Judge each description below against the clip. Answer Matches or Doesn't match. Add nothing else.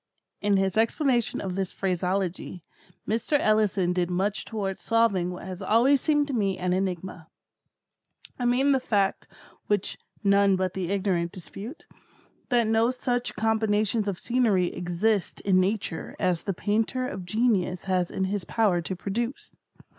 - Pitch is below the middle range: Doesn't match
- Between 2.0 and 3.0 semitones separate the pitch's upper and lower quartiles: Doesn't match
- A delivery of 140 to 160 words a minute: Matches